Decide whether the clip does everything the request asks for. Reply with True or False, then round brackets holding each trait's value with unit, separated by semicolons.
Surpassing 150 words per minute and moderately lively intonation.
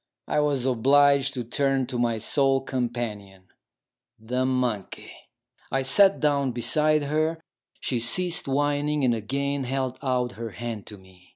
False (145 wpm; 3.2 semitones)